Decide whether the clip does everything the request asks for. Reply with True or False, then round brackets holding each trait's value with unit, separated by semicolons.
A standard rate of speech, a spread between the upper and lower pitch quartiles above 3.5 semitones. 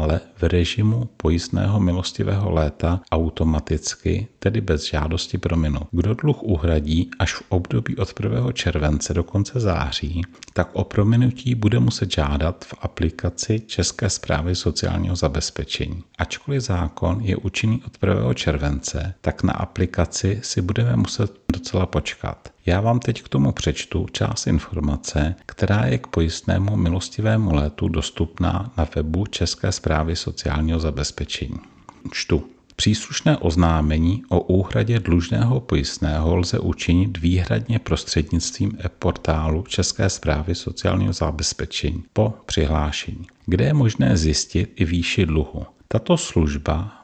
True (125 wpm; 4.3 semitones)